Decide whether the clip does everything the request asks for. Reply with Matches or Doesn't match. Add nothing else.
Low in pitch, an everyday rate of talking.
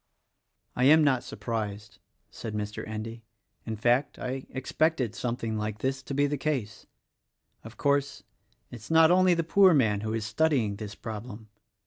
Matches